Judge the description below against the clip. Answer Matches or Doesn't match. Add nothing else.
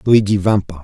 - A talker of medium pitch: Doesn't match